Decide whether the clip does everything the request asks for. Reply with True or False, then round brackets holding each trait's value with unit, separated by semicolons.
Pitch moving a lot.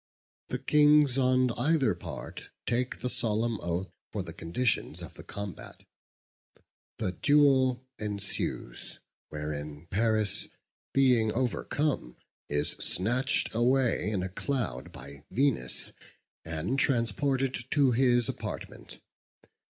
True (5.8 semitones)